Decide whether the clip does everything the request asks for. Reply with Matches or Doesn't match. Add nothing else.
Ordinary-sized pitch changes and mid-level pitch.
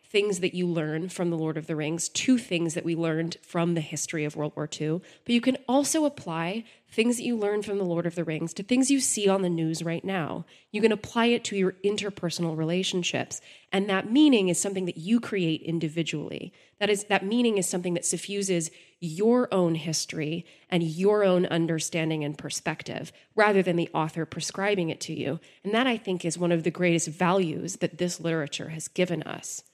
Matches